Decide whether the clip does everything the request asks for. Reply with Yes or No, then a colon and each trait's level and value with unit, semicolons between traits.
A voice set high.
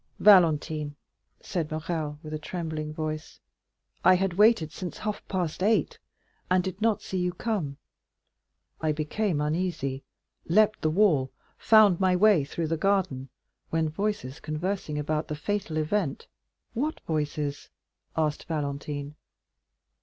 No: medium, 160 Hz